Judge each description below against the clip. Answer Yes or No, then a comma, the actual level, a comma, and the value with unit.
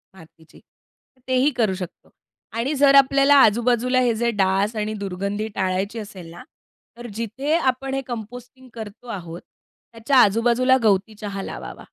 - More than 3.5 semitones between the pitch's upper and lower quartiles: Yes, average, 4.3 semitones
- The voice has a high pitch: Yes, high, 225 Hz